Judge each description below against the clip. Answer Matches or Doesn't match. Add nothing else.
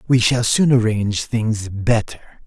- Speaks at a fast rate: Doesn't match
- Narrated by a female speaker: Doesn't match